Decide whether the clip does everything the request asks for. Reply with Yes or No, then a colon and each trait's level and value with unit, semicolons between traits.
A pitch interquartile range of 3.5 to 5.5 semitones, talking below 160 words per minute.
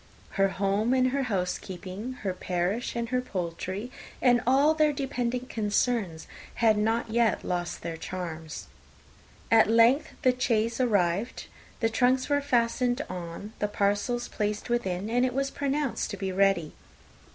Yes: average, 4.6 semitones; average, 145 wpm